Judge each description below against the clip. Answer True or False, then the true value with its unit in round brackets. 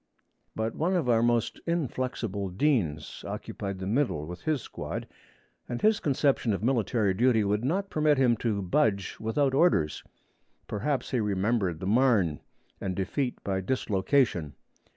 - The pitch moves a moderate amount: False (5.8 semitones)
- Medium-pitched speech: False (115 Hz)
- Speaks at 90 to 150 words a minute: True (145 wpm)